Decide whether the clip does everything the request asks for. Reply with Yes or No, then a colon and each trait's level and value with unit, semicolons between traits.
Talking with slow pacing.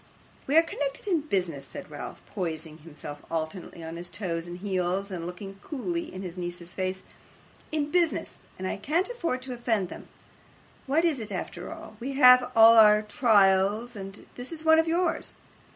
No: average, 180 wpm